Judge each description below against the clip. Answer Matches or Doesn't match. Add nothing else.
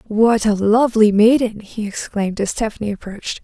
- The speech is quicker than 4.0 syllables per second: Matches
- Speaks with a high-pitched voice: Matches